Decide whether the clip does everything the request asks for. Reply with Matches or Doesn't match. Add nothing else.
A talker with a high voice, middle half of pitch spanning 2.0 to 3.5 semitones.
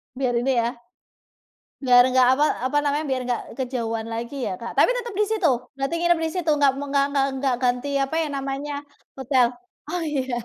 Matches